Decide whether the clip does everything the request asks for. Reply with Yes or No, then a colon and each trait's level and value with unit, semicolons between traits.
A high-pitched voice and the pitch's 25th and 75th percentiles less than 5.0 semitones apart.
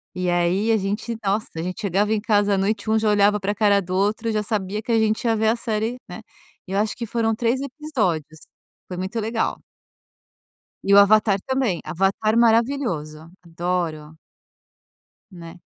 Yes: high, 210 Hz; average, 3.4 semitones